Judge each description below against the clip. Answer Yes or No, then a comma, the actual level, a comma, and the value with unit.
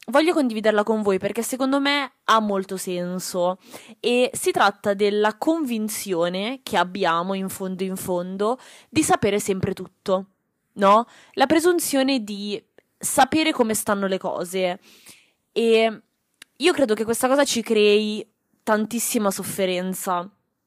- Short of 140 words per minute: Yes, average, 130 wpm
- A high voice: Yes, high, 215 Hz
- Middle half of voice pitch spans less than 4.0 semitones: No, average, 4.5 semitones